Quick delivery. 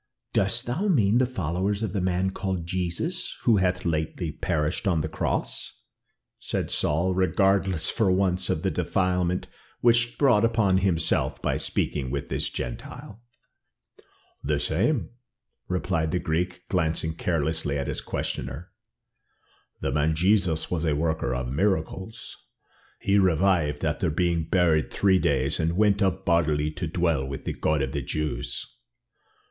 No: average, 145 wpm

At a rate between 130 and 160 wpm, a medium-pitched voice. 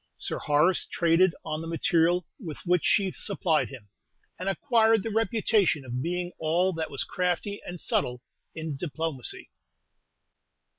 Yes: average, 140 wpm; medium, 170 Hz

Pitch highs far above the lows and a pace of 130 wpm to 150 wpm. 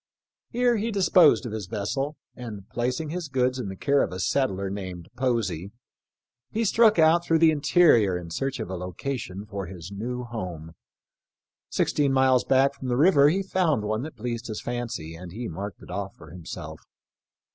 No: wide, 6.9 semitones; average, 180 wpm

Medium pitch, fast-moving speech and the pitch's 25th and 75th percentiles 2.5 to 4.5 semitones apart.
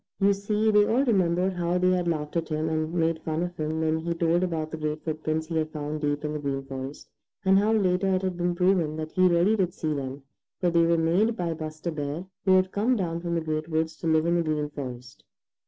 Yes: medium, 165 Hz; fast, 250 wpm; average, 2.8 semitones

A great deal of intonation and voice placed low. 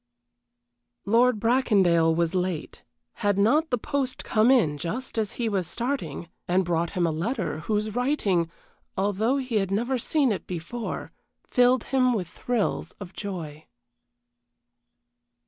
No: wide, 5.9 semitones; high, 210 Hz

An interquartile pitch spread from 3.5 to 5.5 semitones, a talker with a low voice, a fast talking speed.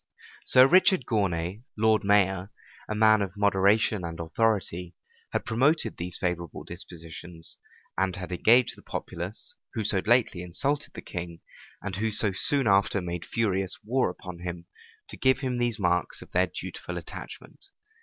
No: average, 4.1 semitones; low, 100 Hz; average, 155 wpm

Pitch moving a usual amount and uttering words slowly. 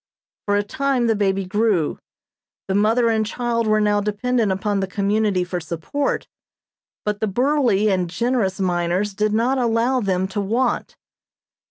No: average, 3.3 semitones; average, 155 wpm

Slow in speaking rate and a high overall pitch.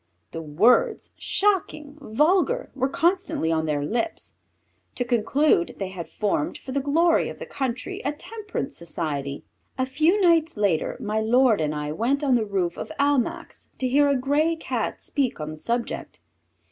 No: average, 165 wpm; very high, 260 Hz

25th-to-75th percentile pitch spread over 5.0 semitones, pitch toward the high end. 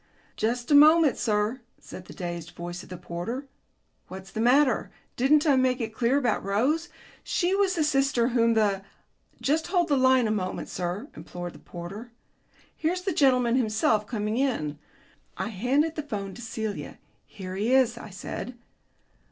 Yes: wide, 5.6 semitones; high, 235 Hz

